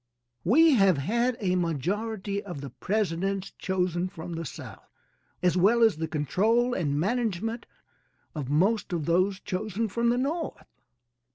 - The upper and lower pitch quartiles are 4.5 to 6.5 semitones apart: Yes, average, 5.0 semitones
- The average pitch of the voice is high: Yes, high, 195 Hz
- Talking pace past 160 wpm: No, average, 145 wpm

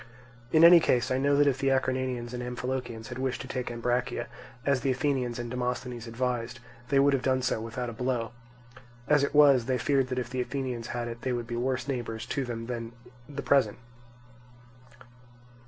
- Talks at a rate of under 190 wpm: No, average, 195 wpm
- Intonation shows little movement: Yes, narrow, 1.8 semitones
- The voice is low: Yes, low, 125 Hz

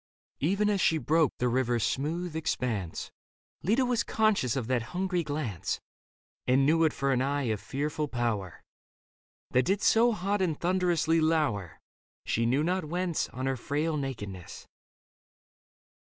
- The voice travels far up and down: Yes, wide, 5.9 semitones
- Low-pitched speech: No, medium, 150 Hz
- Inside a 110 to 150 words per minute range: Yes, average, 145 wpm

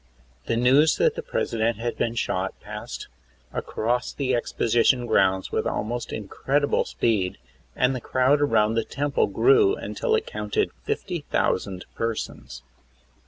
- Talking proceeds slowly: Yes, slow, 130 wpm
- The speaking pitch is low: Yes, low, 120 Hz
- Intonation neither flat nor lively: Yes, average, 4.6 semitones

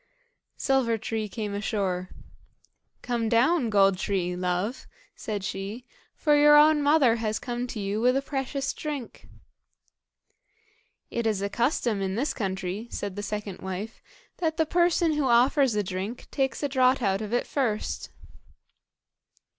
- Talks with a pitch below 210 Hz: No, high, 230 Hz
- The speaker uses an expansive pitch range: No, average, 5.0 semitones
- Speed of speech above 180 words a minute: No, average, 145 wpm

